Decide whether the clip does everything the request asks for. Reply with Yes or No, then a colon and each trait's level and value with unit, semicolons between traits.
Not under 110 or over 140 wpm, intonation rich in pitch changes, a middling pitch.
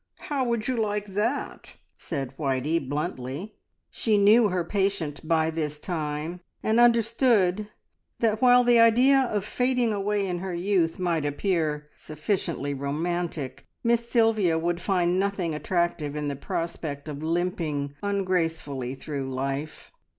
Yes: slow, 135 wpm; wide, 5.7 semitones; medium, 175 Hz